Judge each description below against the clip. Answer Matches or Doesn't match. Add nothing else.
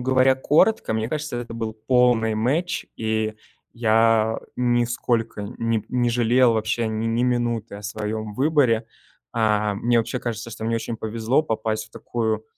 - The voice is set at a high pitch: Doesn't match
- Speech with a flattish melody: Matches